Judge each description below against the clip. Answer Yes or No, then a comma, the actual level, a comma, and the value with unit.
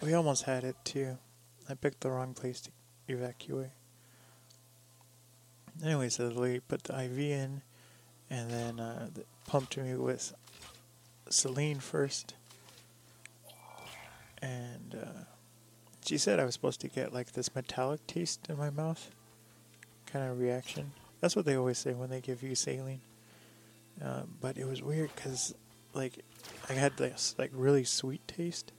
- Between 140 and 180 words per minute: Yes, average, 145 wpm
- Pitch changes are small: Yes, narrow, 2.3 semitones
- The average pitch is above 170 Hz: No, low, 125 Hz